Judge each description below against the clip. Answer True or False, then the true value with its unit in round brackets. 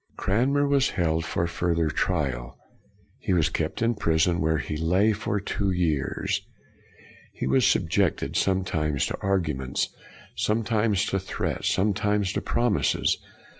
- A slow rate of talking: True (130 wpm)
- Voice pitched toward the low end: True (95 Hz)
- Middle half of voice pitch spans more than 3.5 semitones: True (4.5 semitones)